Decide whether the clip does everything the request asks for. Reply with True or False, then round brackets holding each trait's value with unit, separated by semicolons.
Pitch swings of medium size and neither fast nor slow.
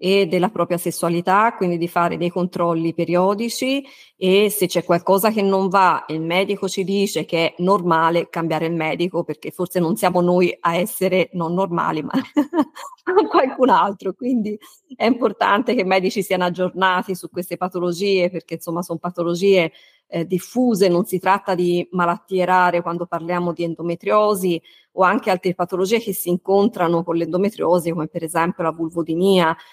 False (2.3 semitones; 160 wpm)